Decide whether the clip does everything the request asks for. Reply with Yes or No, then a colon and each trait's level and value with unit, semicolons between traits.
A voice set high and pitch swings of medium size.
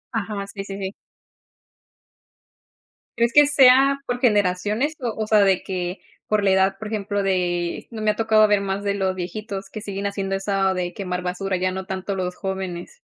No: high, 195 Hz; narrow, 2.2 semitones